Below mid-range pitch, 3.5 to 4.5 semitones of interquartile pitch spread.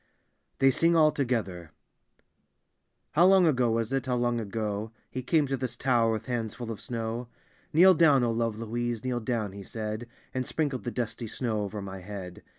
No: low, 120 Hz; average, 3.0 semitones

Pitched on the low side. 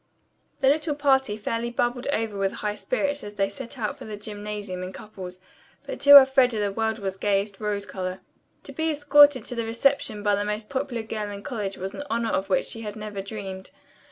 No: high, 215 Hz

